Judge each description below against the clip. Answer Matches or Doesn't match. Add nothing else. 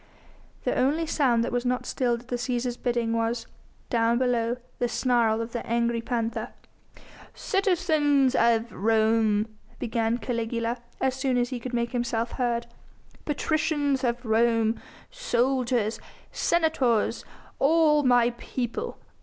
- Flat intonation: Matches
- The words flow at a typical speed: Doesn't match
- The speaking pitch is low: Doesn't match